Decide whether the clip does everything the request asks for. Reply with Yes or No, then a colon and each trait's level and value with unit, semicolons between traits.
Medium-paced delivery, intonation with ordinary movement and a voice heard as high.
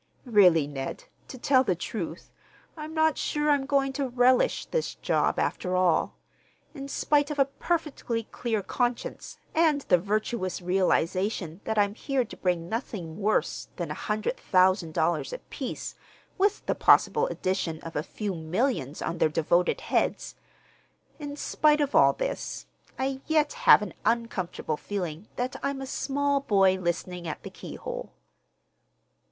No: average, 145 wpm; wide, 7.7 semitones; high, 220 Hz